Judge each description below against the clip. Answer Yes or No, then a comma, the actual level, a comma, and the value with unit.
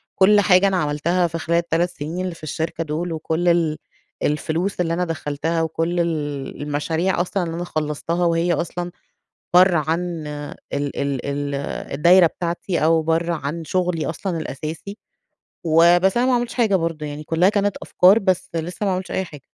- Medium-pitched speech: Yes, medium, 170 Hz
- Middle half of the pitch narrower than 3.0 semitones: Yes, narrow, 2.5 semitones